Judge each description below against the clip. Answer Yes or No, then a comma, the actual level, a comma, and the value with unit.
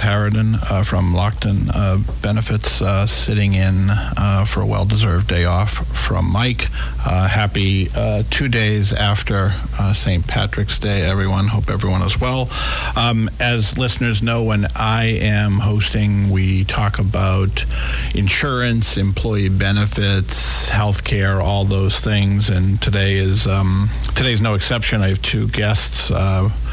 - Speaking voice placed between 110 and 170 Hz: No, low, 100 Hz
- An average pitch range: No, narrow, 2.1 semitones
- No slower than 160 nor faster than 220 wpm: No, average, 145 wpm